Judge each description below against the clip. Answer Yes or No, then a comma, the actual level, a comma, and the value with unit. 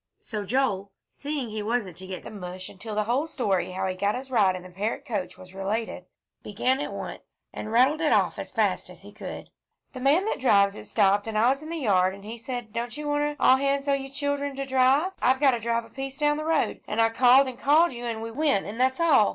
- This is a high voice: Yes, high, 245 Hz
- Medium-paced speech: No, fast, 255 wpm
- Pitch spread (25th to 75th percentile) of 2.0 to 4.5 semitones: No, average, 5.0 semitones